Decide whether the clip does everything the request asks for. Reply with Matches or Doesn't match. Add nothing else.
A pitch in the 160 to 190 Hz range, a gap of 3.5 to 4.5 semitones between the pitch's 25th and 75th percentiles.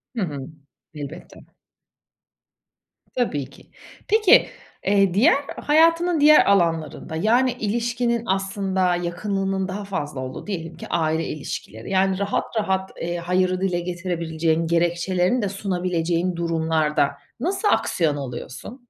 Matches